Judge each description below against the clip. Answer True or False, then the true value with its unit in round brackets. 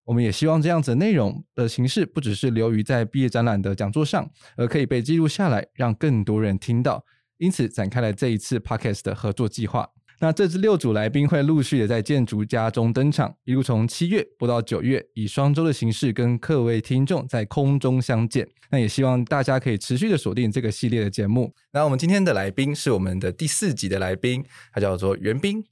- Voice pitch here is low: True (125 Hz)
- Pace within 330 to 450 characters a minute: True (345 characters per minute)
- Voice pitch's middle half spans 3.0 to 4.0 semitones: False (4.4 semitones)